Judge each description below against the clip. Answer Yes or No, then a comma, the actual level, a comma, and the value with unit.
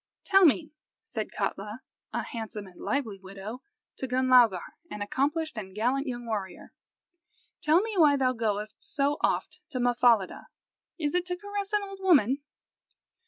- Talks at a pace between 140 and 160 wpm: Yes, average, 150 wpm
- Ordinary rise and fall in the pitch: No, wide, 6.6 semitones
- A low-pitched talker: No, very high, 255 Hz